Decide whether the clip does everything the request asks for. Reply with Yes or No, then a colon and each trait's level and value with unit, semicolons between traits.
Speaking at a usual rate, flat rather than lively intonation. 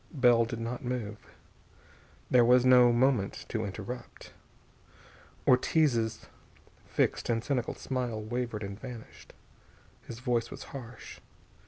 No: slow, 115 wpm; narrow, 1.9 semitones